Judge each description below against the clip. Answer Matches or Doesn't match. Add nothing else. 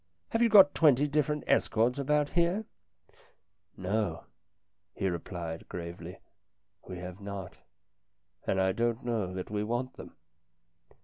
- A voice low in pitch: Matches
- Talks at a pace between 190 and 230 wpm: Doesn't match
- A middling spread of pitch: Doesn't match